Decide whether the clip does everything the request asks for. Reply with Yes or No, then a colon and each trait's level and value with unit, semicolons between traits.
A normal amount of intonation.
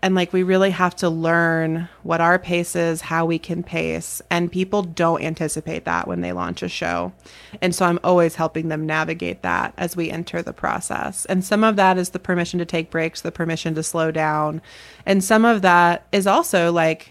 No: narrow, 2.2 semitones